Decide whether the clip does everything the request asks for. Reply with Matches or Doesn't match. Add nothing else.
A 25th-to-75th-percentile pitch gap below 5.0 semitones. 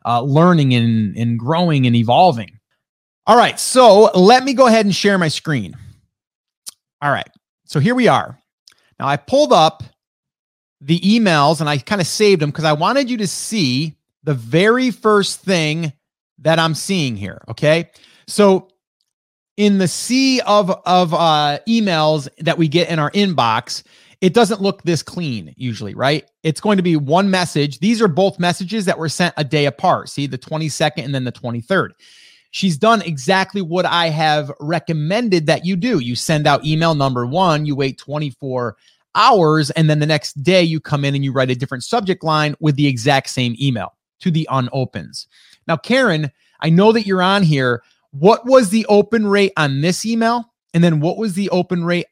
Doesn't match